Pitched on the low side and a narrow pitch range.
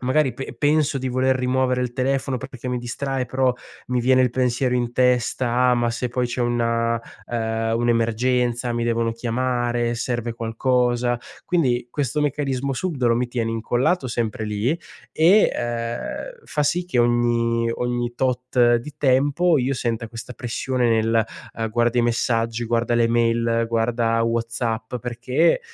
Yes: low, 120 Hz; narrow, 1.7 semitones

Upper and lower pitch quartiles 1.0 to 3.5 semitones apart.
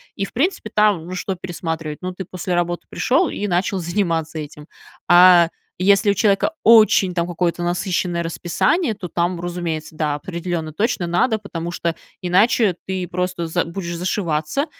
Yes: narrow, 2.6 semitones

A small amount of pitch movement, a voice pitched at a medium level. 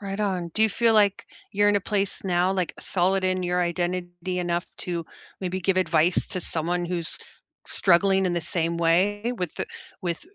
Yes: narrow, 2.0 semitones; medium, 180 Hz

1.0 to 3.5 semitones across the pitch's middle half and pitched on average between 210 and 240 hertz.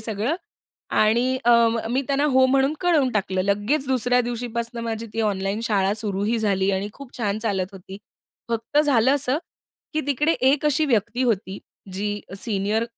No: average, 4.2 semitones; high, 230 Hz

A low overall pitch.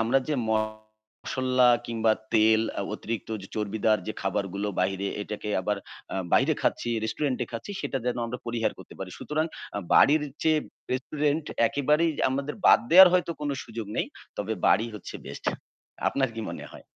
Yes: low, 115 Hz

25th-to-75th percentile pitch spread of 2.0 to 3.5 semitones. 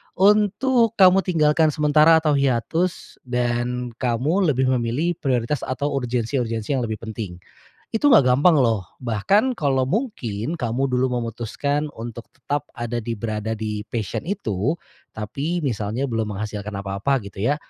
No: average, 5.2 semitones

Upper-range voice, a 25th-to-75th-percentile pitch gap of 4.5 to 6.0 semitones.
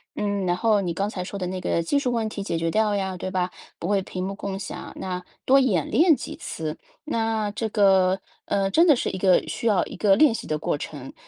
No: high, 195 Hz; average, 3.2 semitones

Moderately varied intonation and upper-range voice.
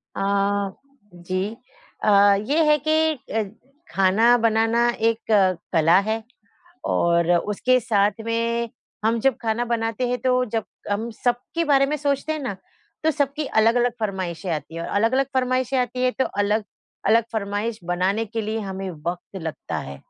Yes: average, 3.9 semitones; high, 225 Hz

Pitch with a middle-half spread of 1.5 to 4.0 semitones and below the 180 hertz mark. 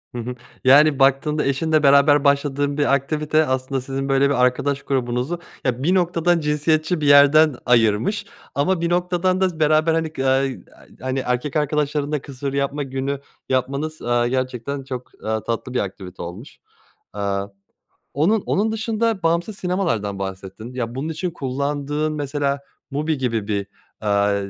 Yes: average, 3.5 semitones; medium, 140 Hz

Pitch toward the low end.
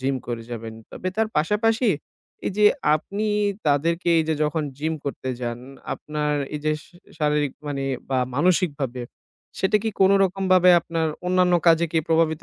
No: medium, 160 Hz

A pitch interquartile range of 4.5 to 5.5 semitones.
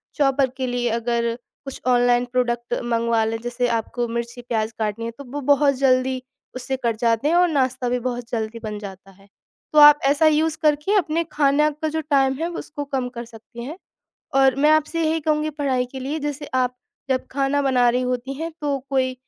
No: average, 3.5 semitones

